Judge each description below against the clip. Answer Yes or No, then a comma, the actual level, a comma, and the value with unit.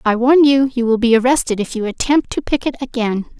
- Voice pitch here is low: No, high, 245 Hz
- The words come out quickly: Yes, fast, 230 wpm